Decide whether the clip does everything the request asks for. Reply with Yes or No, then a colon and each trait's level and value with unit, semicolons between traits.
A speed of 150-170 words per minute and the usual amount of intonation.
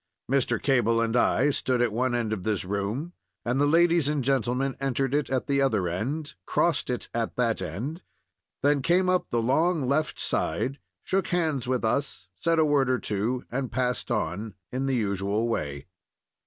No: average, 185 wpm; average, 4.1 semitones